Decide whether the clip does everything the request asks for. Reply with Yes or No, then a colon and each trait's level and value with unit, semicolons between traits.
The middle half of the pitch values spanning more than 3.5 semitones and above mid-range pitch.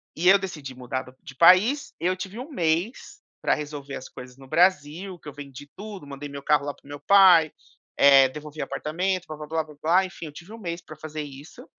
No: average, 4.4 semitones; medium, 155 Hz